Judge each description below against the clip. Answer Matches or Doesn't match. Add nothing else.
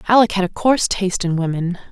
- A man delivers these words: Doesn't match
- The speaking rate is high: Matches